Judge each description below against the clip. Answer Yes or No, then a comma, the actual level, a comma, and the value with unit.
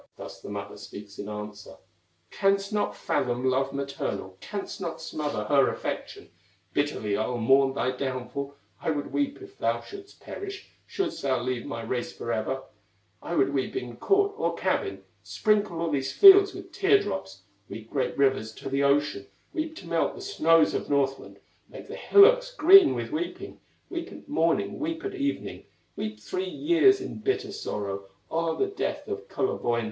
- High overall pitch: No, medium, 150 Hz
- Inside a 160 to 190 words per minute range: Yes, average, 170 wpm